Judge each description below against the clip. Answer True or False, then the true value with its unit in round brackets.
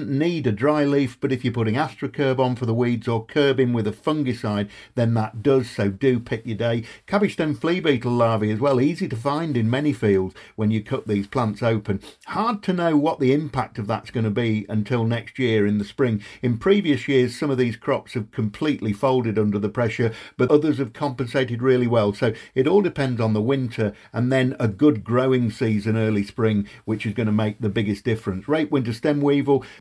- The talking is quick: True (215 wpm)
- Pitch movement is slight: False (4.1 semitones)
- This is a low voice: True (120 Hz)